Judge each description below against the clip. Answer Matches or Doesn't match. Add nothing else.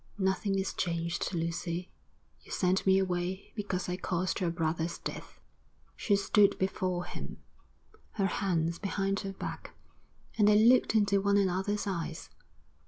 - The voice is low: Doesn't match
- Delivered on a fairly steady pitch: Matches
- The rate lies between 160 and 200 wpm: Doesn't match